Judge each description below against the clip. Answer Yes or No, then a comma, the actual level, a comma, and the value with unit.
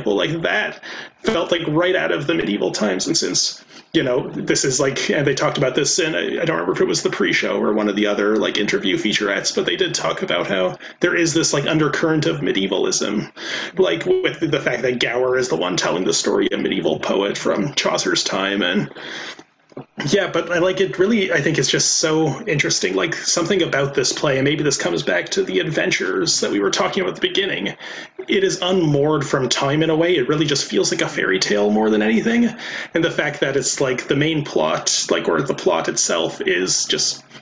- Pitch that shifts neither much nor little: No, wide, 5.9 semitones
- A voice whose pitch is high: No, medium, 155 Hz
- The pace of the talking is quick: Yes, fast, 225 wpm